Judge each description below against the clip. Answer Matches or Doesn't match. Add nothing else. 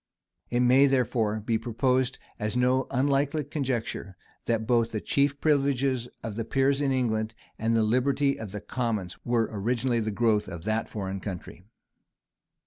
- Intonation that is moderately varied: Matches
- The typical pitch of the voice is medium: Doesn't match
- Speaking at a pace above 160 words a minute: Doesn't match